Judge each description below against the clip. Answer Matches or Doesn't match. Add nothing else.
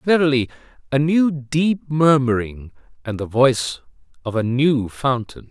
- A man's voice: Matches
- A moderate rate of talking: Doesn't match